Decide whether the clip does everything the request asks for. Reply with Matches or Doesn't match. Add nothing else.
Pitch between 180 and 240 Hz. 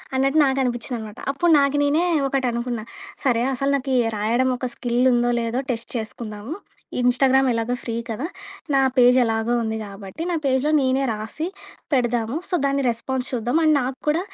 Doesn't match